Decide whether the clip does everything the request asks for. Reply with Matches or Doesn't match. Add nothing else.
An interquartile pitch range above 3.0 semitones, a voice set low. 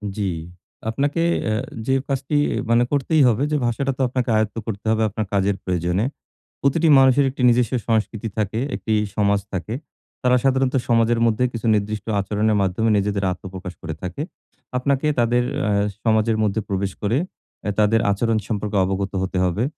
Matches